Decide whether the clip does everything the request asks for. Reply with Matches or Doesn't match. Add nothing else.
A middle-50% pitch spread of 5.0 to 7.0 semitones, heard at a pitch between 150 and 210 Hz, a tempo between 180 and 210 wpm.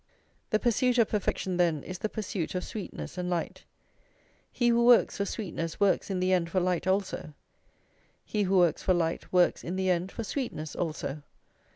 Doesn't match